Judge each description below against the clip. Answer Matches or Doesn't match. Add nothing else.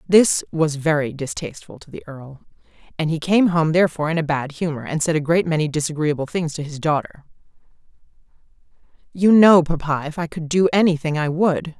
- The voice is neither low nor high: Matches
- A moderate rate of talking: Matches